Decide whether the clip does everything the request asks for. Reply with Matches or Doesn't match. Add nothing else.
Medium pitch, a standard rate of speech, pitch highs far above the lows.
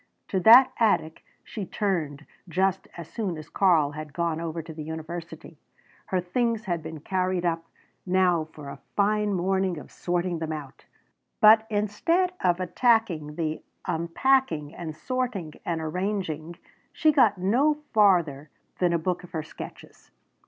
Doesn't match